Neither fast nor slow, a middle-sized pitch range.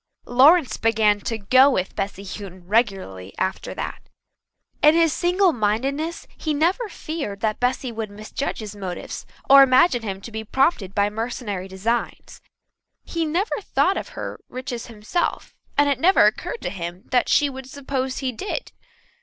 No: average, 160 wpm; wide, 5.8 semitones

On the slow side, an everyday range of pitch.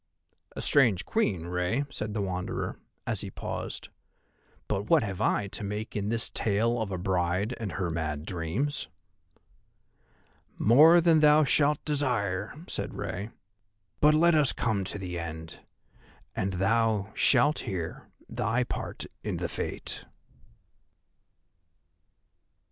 No: slow, 130 wpm; wide, 6.7 semitones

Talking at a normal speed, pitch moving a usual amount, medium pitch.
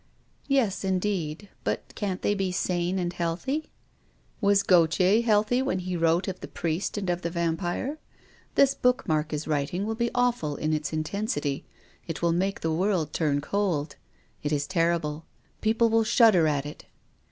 Yes: average, 175 wpm; average, 4.6 semitones; medium, 180 Hz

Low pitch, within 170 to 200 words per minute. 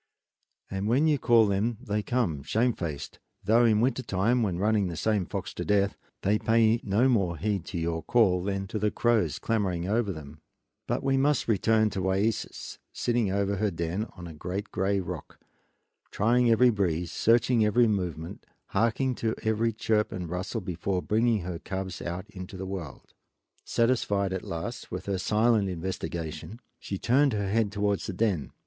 Yes: low, 100 Hz; average, 175 wpm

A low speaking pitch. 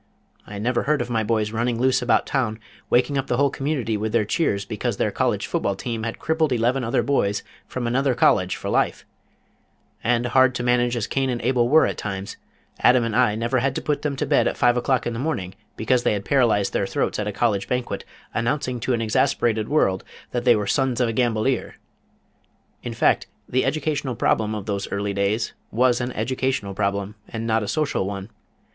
Yes: low, 120 Hz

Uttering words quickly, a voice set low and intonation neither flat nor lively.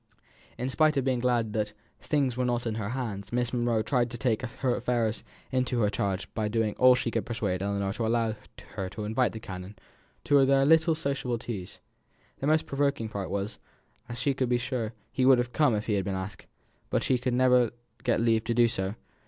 Yes: fast, 210 wpm; low, 120 Hz; average, 3.1 semitones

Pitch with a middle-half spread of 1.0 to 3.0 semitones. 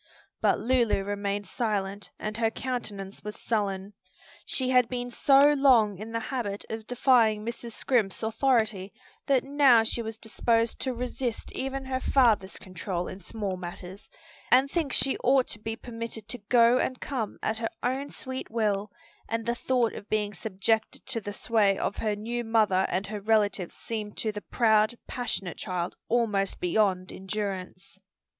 No: average, 3.4 semitones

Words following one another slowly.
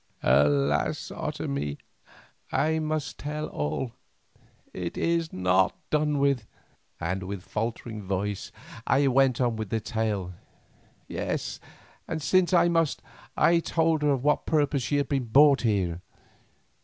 Yes: slow, 130 wpm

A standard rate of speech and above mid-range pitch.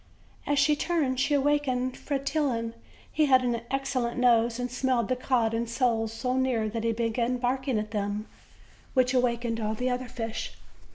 Yes: average, 175 wpm; very high, 250 Hz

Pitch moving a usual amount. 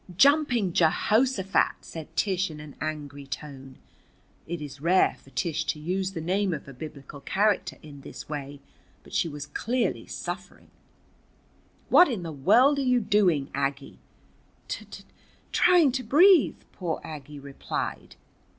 No: wide, 6.8 semitones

